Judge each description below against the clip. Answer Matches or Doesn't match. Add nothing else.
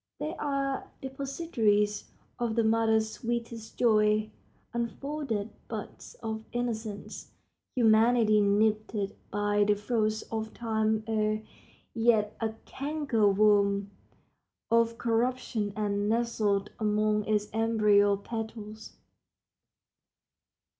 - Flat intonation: Matches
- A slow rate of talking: Matches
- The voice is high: Matches